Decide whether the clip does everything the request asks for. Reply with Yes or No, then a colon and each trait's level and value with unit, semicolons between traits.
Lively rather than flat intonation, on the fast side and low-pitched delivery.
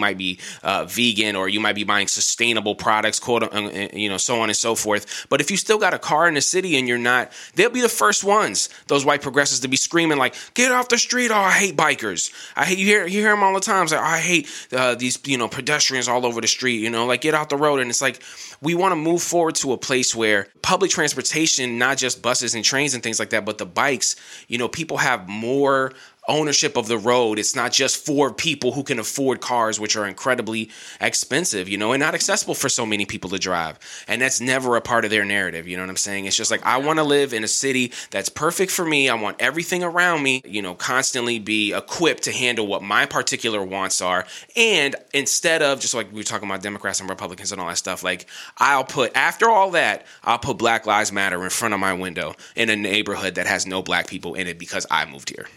Yes: wide, 6.0 semitones; fast, 250 wpm; low, 120 Hz